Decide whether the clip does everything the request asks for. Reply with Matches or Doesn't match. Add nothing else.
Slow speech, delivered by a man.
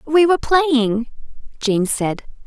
Doesn't match